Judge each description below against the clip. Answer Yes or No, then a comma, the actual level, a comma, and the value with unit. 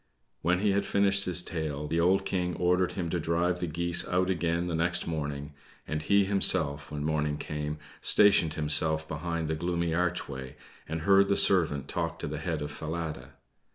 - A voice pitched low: Yes, very low, 85 Hz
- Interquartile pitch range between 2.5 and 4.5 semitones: Yes, average, 2.8 semitones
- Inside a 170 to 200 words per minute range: Yes, average, 185 wpm